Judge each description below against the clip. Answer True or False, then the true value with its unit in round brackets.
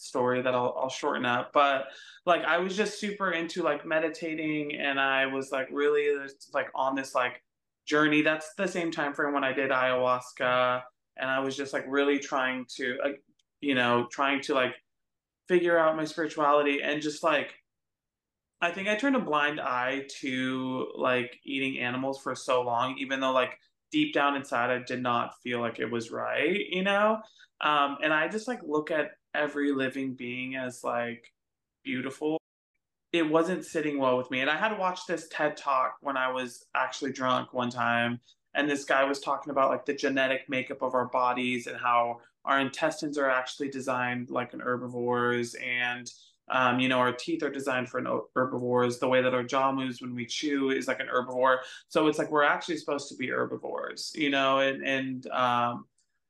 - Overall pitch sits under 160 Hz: True (135 Hz)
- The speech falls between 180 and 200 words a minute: True (190 wpm)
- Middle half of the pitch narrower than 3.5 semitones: True (3.0 semitones)